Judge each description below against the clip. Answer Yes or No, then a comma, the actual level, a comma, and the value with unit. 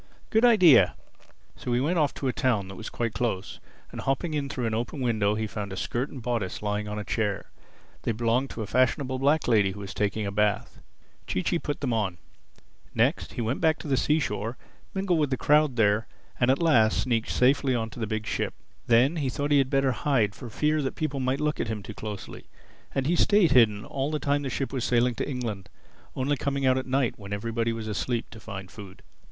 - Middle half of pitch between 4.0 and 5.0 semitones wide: Yes, average, 4.5 semitones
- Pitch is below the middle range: Yes, low, 120 Hz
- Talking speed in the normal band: No, fast, 225 wpm